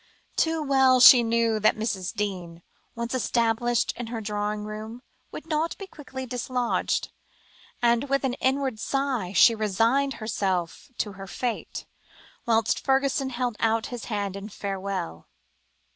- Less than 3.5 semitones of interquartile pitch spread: No, average, 3.9 semitones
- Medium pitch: No, high, 230 Hz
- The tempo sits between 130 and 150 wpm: Yes, average, 140 wpm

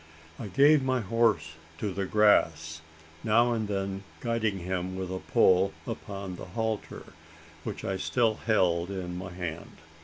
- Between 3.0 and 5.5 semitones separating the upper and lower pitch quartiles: Yes, average, 3.5 semitones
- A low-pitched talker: Yes, very low, 95 Hz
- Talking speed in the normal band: Yes, average, 150 wpm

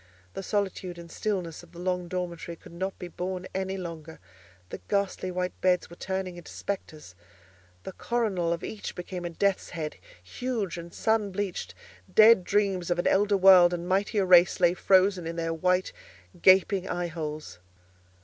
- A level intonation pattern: Yes, narrow, 2.2 semitones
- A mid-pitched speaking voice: Yes, medium, 180 Hz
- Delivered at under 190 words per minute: Yes, average, 160 wpm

